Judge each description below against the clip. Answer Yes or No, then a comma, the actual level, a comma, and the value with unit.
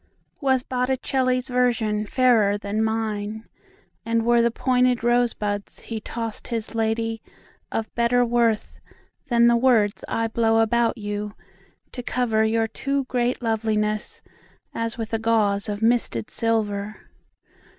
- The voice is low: No, high, 225 Hz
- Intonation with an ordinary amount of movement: No, narrow, 2.0 semitones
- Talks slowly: Yes, slow, 100 wpm